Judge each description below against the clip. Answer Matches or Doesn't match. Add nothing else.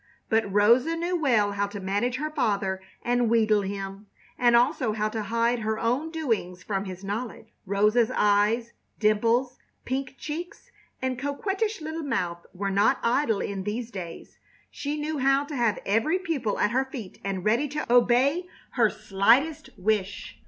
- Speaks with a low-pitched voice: Doesn't match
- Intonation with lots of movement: Doesn't match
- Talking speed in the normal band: Matches